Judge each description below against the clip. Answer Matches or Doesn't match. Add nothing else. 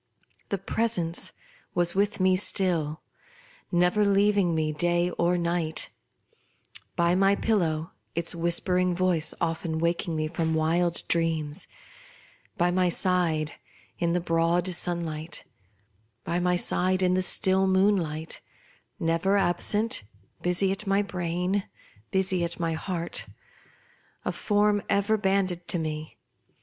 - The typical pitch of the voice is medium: Matches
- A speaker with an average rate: Doesn't match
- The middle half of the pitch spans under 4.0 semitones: Matches